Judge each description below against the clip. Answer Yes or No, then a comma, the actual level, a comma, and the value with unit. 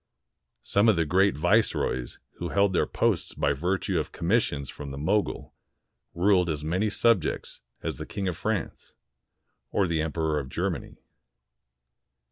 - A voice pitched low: Yes, very low, 90 Hz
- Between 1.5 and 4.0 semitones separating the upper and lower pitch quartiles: No, average, 4.6 semitones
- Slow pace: No, average, 145 wpm